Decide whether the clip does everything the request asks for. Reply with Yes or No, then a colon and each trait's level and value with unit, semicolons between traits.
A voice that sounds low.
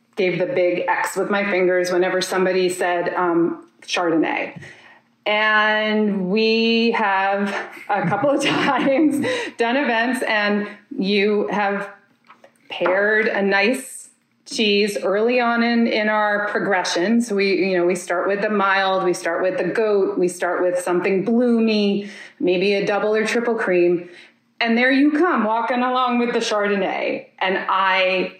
No: high, 205 Hz